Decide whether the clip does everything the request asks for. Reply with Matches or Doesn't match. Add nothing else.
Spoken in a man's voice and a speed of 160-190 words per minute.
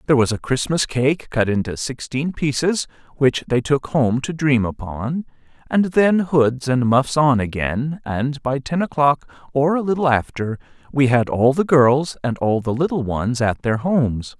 Matches